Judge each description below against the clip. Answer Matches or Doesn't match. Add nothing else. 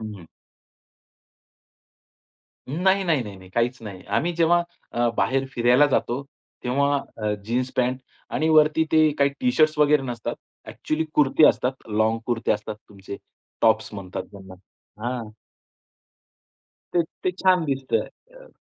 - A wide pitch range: Matches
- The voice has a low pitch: Matches